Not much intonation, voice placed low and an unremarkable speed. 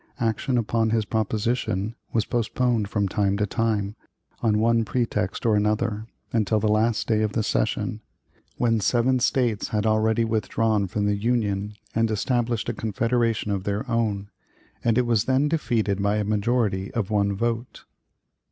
Yes: narrow, 2.1 semitones; low, 110 Hz; average, 160 wpm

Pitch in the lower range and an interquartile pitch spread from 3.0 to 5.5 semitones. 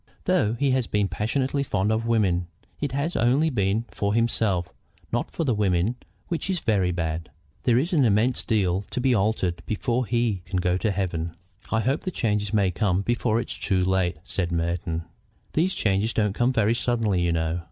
Yes: low, 105 Hz; average, 4.7 semitones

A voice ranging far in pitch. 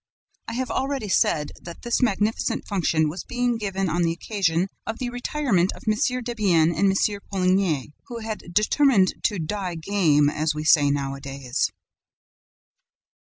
Yes: wide, 5.7 semitones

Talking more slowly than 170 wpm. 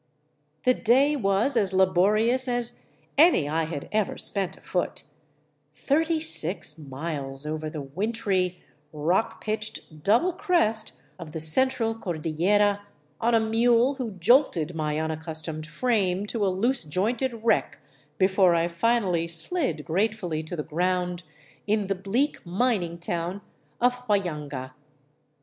Yes: slow, 135 wpm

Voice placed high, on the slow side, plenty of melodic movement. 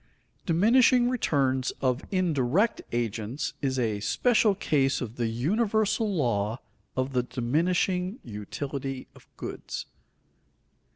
No: medium, 140 Hz; slow, 105 wpm; wide, 7.8 semitones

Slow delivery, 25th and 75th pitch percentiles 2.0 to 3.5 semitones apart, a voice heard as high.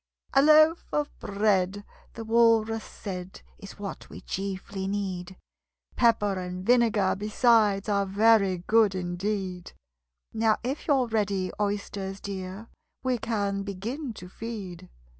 Yes: slow, 120 wpm; average, 3.0 semitones; high, 205 Hz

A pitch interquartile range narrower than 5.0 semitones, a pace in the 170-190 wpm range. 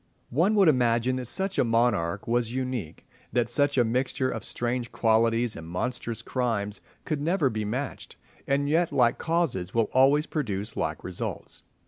No: average, 3.8 semitones; average, 160 wpm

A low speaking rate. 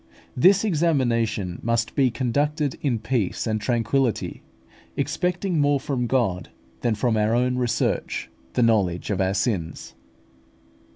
Yes: slow, 125 wpm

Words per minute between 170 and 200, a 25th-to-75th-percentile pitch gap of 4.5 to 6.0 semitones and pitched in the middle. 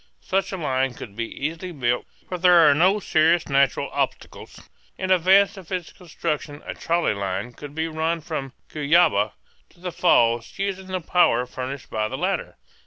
Yes: average, 175 wpm; wide, 5.6 semitones; medium, 160 Hz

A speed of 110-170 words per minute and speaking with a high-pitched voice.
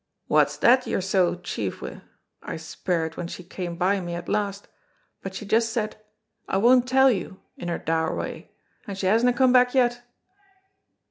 No: average, 180 wpm; high, 195 Hz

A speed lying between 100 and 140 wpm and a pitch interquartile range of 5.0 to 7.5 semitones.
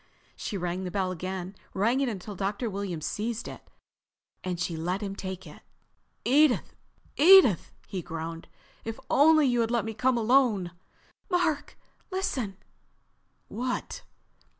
Yes: slow, 135 wpm; wide, 5.6 semitones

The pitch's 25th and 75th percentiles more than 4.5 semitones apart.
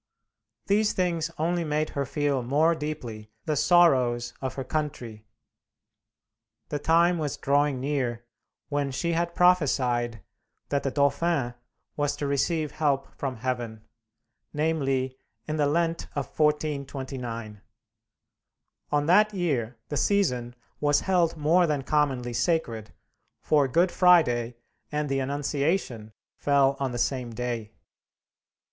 No: average, 4.0 semitones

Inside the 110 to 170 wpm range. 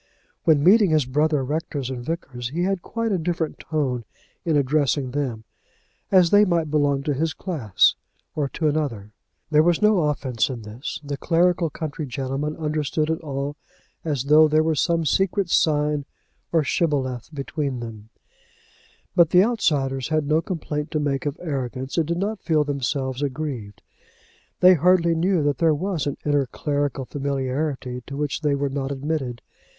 Yes: average, 165 wpm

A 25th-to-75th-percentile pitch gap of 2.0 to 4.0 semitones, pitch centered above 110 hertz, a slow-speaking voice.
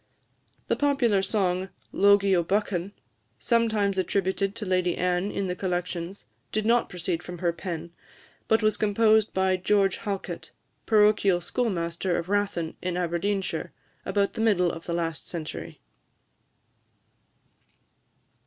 Yes: average, 2.8 semitones; high, 190 Hz; slow, 125 wpm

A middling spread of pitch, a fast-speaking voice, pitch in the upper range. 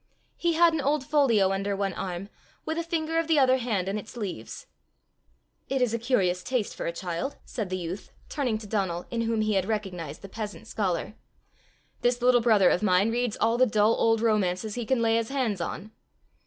Yes: average, 4.3 semitones; fast, 210 wpm; high, 220 Hz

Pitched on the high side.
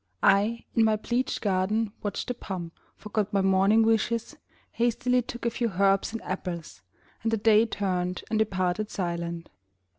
Yes: high, 210 Hz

